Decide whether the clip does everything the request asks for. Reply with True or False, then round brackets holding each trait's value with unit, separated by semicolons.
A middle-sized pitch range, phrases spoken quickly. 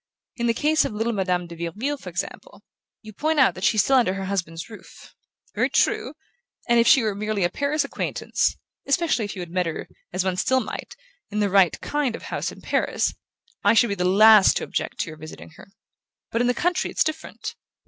False (5.8 semitones; 220 wpm)